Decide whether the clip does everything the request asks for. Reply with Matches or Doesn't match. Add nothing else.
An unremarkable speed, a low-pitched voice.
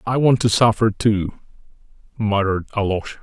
Doesn't match